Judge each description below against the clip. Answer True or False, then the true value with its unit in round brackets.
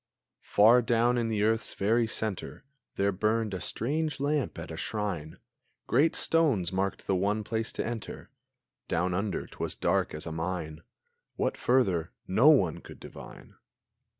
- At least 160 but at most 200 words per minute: False (150 wpm)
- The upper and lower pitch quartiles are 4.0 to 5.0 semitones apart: True (4.4 semitones)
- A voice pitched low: True (105 Hz)